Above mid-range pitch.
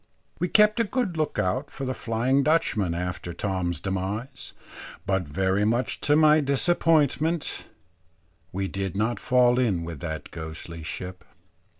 No: low, 115 Hz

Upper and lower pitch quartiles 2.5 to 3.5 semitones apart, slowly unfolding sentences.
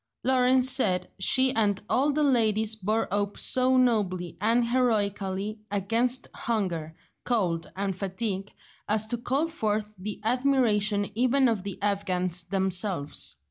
No: average, 4.3 semitones; slow, 130 wpm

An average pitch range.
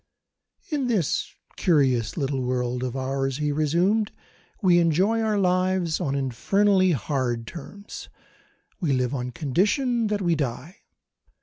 No: wide, 6.7 semitones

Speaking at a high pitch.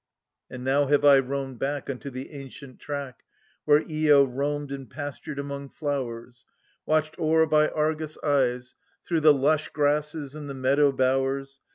No: medium, 140 Hz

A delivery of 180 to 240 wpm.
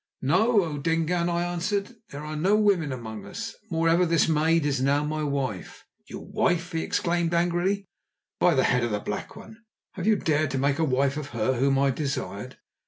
Yes: average, 195 wpm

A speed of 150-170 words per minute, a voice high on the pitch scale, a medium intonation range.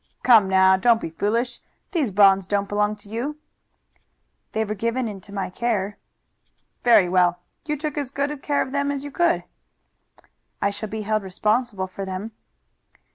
Yes: average, 165 wpm; high, 215 Hz; average, 4.8 semitones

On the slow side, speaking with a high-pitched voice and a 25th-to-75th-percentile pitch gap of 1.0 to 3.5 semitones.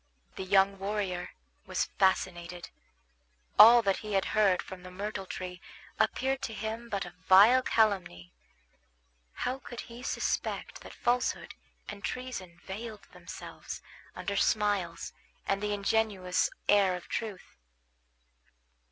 Yes: slow, 125 wpm; high, 200 Hz; average, 2.9 semitones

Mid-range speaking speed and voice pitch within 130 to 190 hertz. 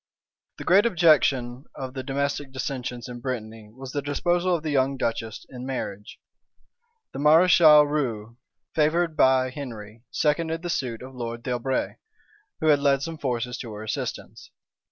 Yes: average, 155 wpm; low, 135 Hz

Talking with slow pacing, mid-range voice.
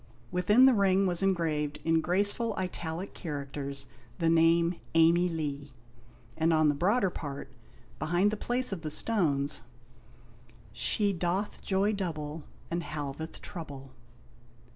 Yes: slow, 125 wpm; medium, 170 Hz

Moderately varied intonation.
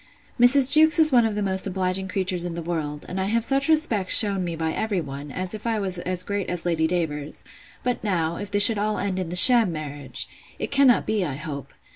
Yes: average, 4.6 semitones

